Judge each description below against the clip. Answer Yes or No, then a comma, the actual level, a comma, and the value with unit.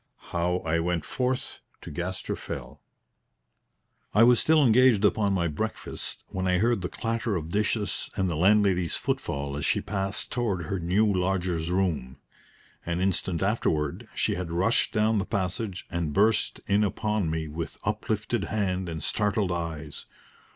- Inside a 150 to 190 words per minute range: Yes, average, 160 wpm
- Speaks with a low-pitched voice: Yes, very low, 95 Hz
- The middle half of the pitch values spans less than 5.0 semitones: Yes, average, 3.9 semitones